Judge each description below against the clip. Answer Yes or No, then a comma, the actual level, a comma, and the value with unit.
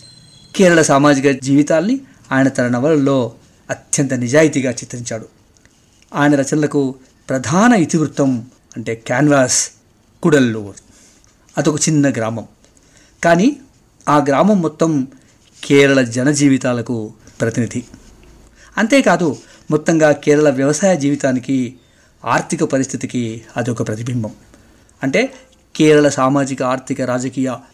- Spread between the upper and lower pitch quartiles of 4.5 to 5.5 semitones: No, average, 3.6 semitones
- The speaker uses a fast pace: No, average, 90 wpm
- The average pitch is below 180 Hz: Yes, low, 135 Hz